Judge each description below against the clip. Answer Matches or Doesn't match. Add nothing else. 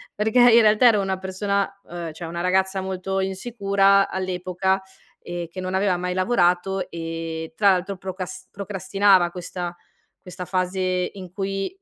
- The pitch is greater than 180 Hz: Matches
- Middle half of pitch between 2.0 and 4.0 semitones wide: Doesn't match